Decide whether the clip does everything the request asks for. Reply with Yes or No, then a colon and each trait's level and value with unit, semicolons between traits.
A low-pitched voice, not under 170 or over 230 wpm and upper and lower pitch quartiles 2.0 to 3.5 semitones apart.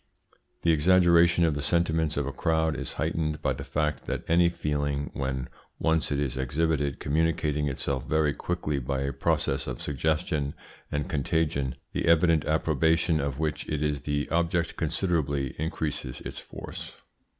No: very low, 75 Hz; average, 155 wpm; narrow, 2.5 semitones